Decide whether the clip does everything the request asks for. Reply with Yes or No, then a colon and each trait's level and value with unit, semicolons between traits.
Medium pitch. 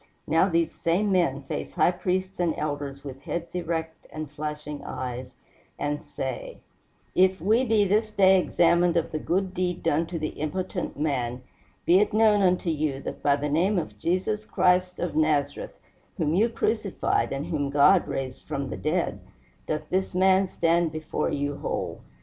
Yes: medium, 170 Hz